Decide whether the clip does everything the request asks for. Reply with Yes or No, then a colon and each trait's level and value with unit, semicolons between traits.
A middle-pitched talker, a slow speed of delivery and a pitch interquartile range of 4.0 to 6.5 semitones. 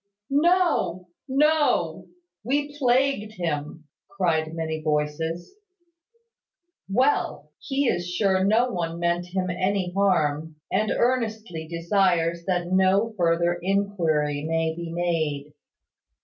Yes: medium, 180 Hz; slow, 105 wpm; average, 4.5 semitones